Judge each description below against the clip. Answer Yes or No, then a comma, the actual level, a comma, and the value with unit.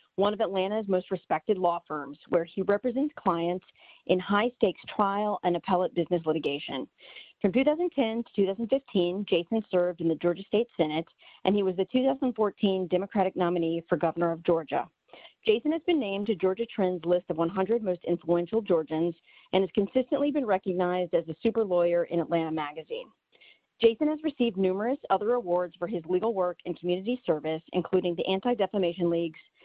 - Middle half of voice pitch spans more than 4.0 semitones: Yes, average, 4.6 semitones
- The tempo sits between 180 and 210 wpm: No, average, 170 wpm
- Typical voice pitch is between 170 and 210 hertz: Yes, medium, 185 Hz